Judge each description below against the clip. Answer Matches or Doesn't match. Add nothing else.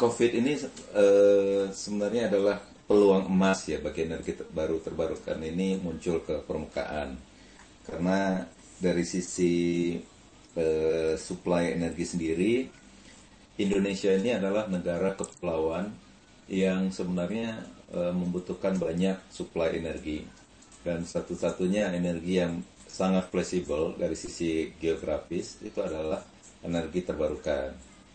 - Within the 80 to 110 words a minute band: Matches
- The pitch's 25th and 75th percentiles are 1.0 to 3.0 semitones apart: Matches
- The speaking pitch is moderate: Doesn't match